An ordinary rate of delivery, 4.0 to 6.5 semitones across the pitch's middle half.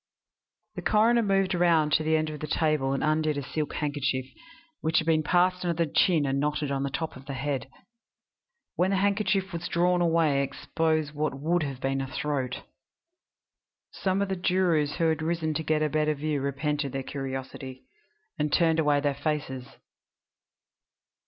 No: average, 180 wpm; average, 3.3 semitones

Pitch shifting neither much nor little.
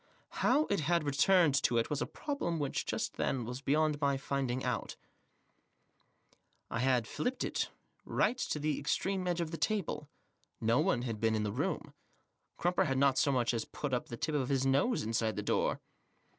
Yes: average, 5.0 semitones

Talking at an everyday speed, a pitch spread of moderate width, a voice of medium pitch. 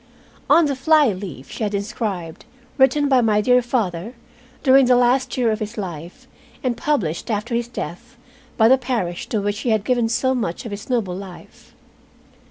No: average, 180 wpm; average, 4.1 semitones; high, 230 Hz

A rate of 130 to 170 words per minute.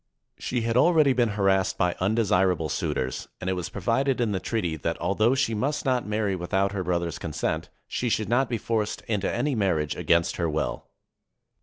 No: average, 185 wpm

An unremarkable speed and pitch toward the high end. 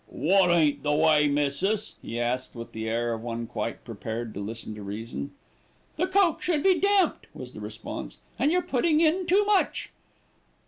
No: average, 180 wpm; medium, 150 Hz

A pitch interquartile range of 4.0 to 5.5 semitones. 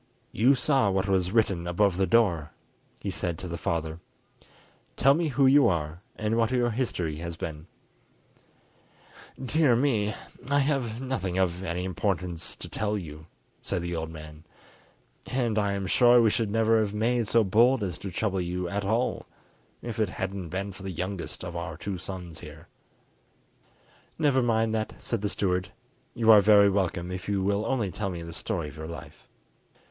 Yes: average, 4.6 semitones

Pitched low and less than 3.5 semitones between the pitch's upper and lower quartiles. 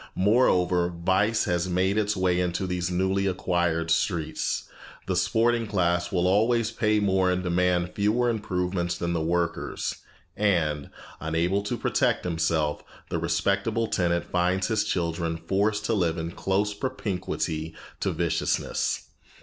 Yes: very low, 90 Hz; average, 2.9 semitones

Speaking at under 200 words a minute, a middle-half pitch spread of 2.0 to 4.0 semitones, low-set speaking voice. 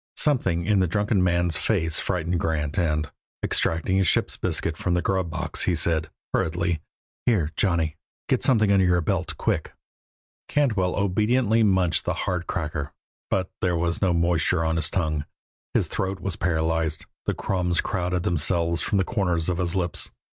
Yes: average, 165 wpm; average, 2.7 semitones; very low, 90 Hz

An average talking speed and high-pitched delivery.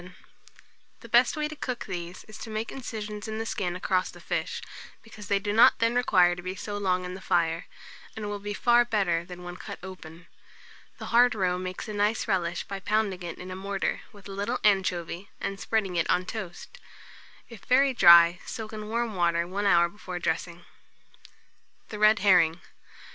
Yes: average, 190 wpm; high, 195 Hz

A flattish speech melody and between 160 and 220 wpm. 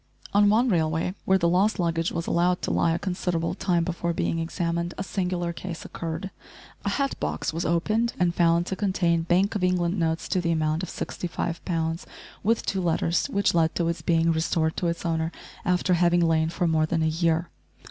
Yes: narrow, 1.7 semitones; average, 200 wpm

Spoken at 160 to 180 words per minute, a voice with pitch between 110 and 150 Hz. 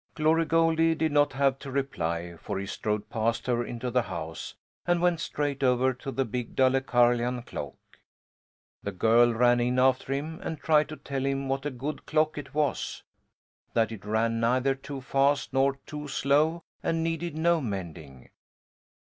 Yes: average, 170 wpm; low, 135 Hz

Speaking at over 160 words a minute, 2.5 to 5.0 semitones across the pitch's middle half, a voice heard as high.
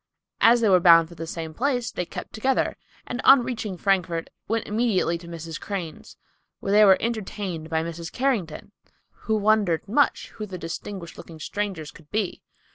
Yes: average, 175 wpm; average, 4.7 semitones; high, 195 Hz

